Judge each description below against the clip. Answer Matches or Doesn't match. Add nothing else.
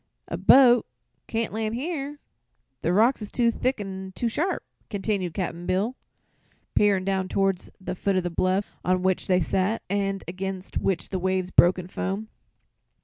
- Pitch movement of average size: Matches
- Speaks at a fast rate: Doesn't match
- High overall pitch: Matches